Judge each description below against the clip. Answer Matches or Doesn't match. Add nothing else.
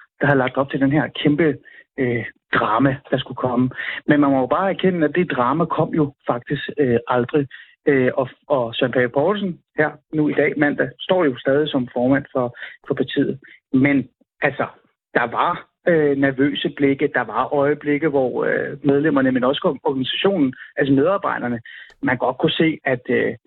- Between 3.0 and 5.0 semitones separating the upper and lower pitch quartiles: Doesn't match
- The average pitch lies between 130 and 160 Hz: Matches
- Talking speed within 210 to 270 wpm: Doesn't match